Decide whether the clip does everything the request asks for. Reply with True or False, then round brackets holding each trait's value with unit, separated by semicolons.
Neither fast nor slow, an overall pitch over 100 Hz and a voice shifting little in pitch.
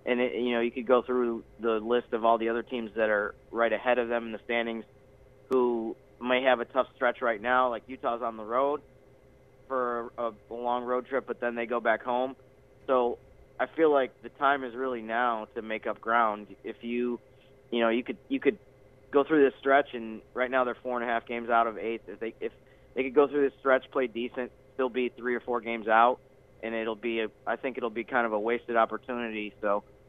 False (235 wpm; 120 Hz; 2.2 semitones)